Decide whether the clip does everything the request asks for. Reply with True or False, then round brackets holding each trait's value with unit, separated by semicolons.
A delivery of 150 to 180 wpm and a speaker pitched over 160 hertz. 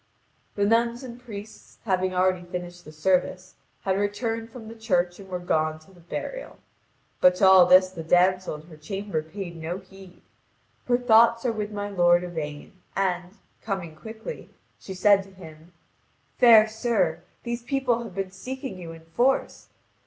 True (165 wpm; 190 Hz)